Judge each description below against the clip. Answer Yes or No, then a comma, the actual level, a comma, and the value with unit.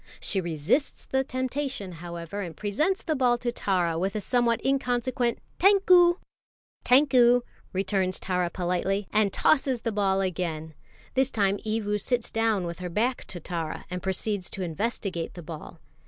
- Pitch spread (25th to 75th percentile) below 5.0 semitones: No, wide, 5.4 semitones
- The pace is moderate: Yes, average, 155 wpm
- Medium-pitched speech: No, high, 205 Hz